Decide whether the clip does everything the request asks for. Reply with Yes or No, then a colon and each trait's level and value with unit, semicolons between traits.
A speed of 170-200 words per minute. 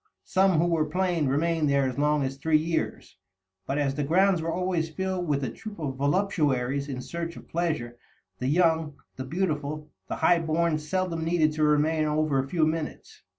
Yes: average, 190 wpm